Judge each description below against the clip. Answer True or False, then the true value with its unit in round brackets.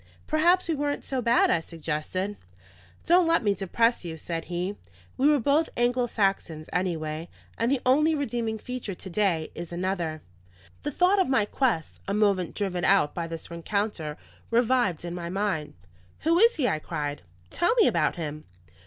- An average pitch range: False (7.4 semitones)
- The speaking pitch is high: True (200 Hz)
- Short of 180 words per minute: True (170 wpm)